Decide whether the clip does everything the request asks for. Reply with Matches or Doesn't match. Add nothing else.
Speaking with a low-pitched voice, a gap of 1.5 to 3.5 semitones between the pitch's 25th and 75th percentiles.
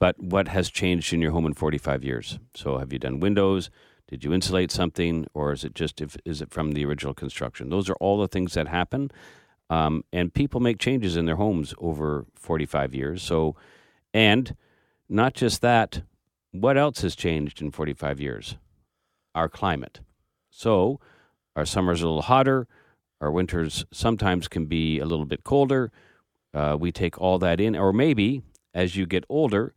Doesn't match